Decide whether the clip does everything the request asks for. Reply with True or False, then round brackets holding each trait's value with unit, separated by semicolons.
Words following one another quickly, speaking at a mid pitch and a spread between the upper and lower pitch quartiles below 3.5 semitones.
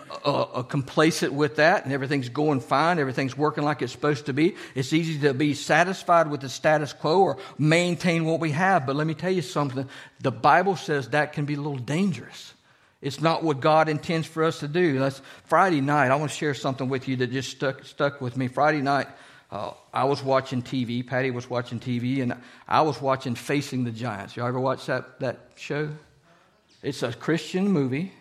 True (210 wpm; 145 Hz; 2.8 semitones)